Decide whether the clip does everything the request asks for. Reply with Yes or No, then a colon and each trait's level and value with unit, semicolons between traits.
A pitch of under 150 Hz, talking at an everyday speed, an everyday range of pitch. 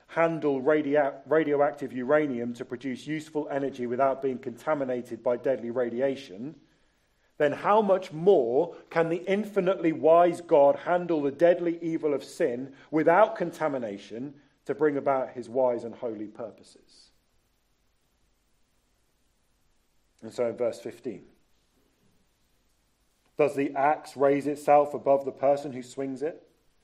No: medium, 140 Hz; slow, 125 wpm; average, 3.9 semitones